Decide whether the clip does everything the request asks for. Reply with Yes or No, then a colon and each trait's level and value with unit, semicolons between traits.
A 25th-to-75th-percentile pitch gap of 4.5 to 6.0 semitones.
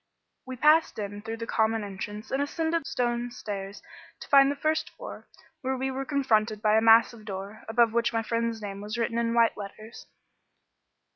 No: average, 3.4 semitones